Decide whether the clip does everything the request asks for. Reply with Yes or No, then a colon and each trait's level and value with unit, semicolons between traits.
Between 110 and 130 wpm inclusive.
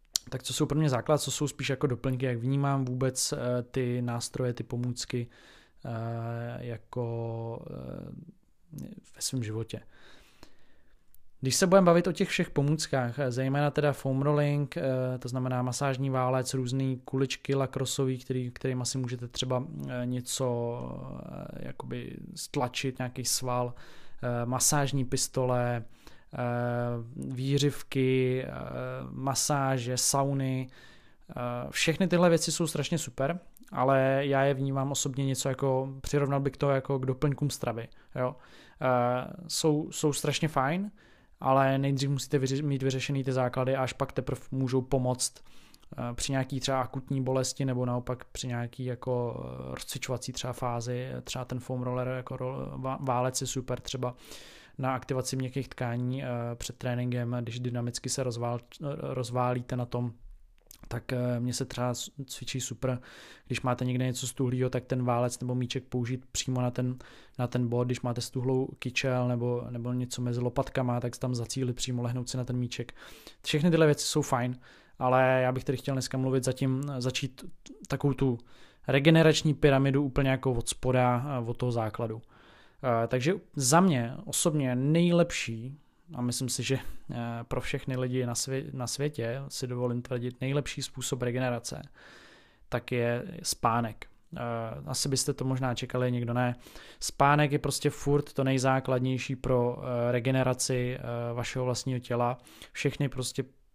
No: average, 140 wpm